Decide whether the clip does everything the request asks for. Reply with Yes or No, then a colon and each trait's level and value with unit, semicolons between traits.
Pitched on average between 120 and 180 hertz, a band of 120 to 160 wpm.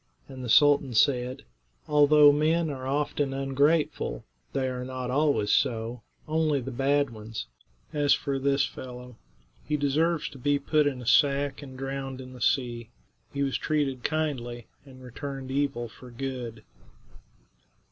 Yes: low, 135 Hz; average, 145 wpm